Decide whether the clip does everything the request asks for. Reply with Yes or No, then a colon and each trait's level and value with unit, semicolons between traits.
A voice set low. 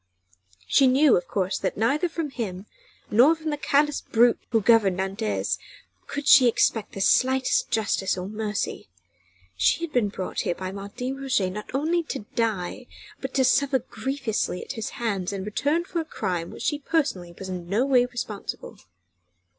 No: high, 230 Hz